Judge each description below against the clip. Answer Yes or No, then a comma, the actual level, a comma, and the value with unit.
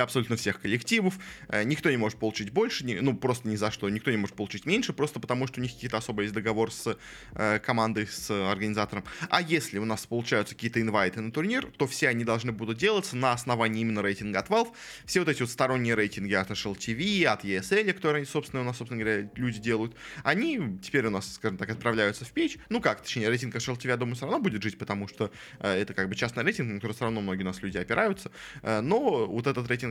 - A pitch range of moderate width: Yes, average, 3.9 semitones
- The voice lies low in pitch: Yes, low, 115 Hz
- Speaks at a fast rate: Yes, fast, 235 wpm